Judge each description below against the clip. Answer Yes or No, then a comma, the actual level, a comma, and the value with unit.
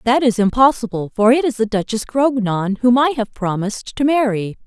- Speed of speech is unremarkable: Yes, average, 195 wpm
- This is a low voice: No, high, 235 Hz